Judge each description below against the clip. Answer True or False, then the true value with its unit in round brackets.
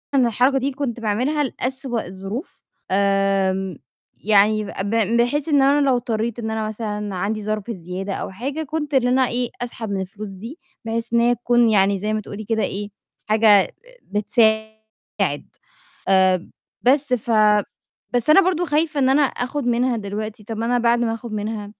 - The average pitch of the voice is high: True (225 Hz)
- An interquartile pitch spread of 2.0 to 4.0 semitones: True (3.4 semitones)